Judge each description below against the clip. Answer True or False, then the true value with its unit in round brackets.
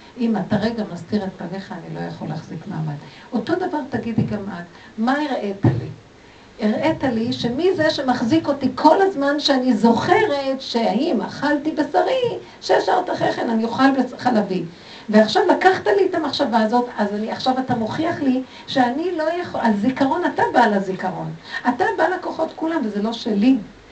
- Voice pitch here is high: True (245 Hz)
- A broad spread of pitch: True (6.2 semitones)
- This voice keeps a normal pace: False (165 wpm)